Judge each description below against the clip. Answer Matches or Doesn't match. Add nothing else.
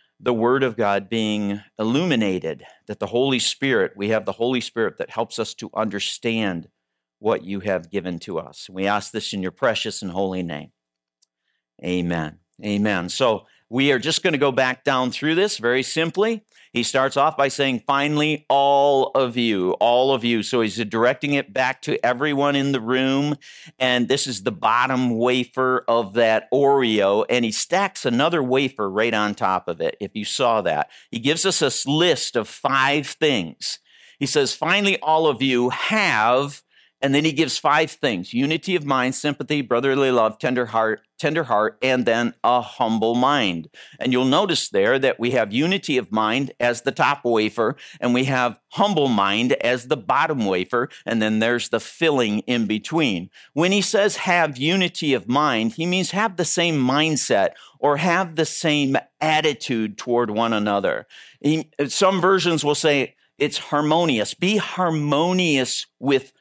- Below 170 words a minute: Doesn't match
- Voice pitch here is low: Matches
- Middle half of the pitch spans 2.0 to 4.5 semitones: Doesn't match